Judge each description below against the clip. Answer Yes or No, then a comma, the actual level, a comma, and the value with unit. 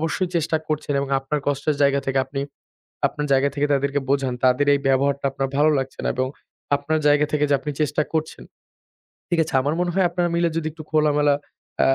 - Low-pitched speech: No, medium, 145 Hz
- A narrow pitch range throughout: Yes, narrow, 2.0 semitones